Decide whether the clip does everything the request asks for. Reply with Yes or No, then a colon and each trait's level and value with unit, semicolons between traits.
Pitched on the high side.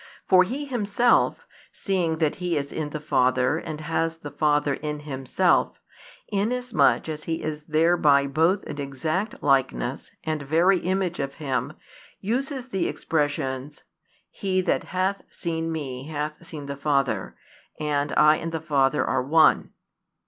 No: medium, 155 Hz